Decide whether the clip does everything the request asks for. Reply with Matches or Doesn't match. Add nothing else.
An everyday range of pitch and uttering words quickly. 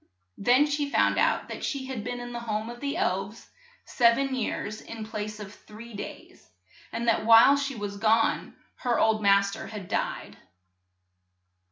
Doesn't match